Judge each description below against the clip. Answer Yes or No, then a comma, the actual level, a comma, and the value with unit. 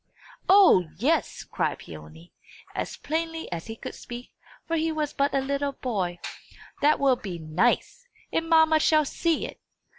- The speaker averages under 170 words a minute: Yes, average, 155 wpm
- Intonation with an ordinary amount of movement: No, wide, 8.7 semitones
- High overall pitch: Yes, very high, 280 Hz